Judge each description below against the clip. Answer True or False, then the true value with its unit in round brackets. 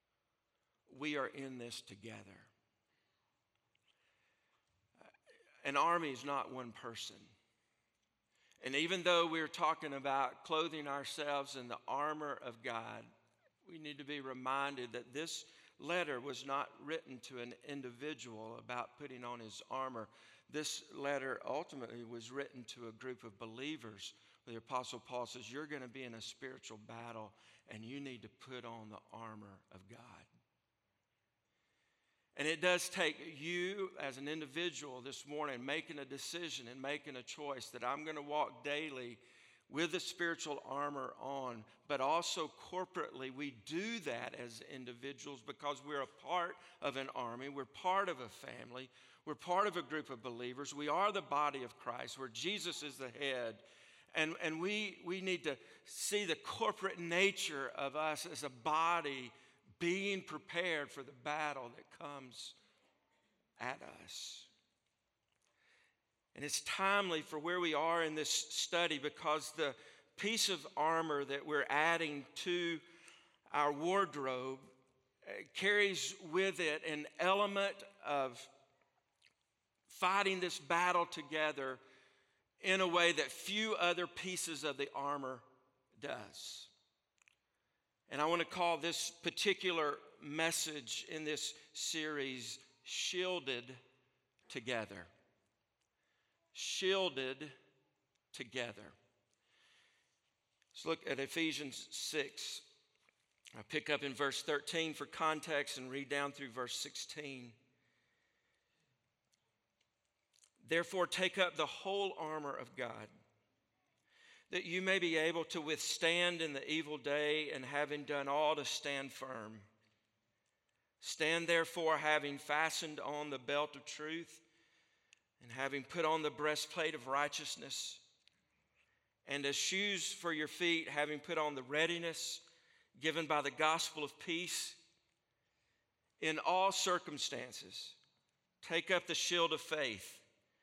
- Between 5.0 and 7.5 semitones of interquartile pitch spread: False (4.3 semitones)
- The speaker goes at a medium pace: False (130 wpm)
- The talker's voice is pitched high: False (150 Hz)